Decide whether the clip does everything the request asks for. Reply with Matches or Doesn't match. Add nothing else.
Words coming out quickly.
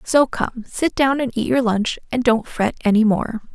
Matches